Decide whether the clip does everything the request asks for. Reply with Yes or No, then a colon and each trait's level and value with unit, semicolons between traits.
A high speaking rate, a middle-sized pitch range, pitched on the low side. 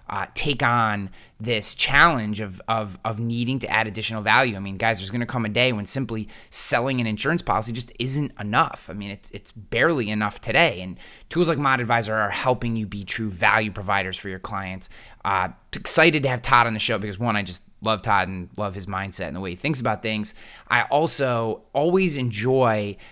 Yes: fast, 215 wpm; average, 3.3 semitones; low, 110 Hz